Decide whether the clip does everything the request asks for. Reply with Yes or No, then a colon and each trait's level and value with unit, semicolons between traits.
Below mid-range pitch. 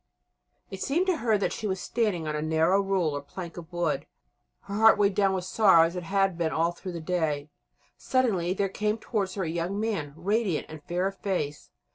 No: medium, 185 Hz